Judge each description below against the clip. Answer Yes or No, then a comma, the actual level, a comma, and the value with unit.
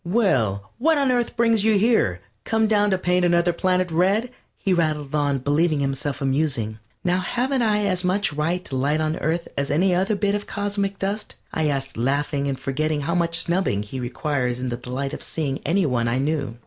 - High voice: No, medium, 160 Hz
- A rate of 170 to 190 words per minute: No, fast, 205 wpm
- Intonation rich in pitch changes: Yes, wide, 6.2 semitones